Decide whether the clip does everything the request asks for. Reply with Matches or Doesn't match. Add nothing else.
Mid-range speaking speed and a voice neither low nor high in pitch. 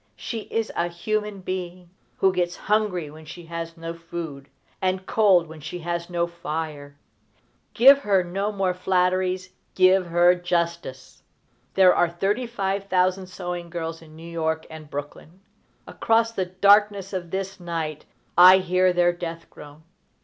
Matches